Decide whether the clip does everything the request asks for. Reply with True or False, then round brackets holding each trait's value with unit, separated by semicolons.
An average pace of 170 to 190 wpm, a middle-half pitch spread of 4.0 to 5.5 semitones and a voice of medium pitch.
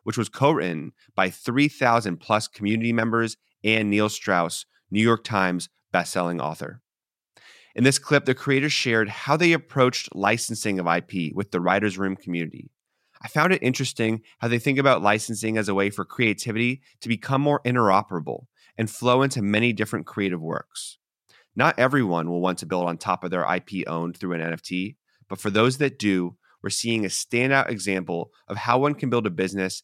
False (185 wpm; 4.7 semitones; 110 Hz)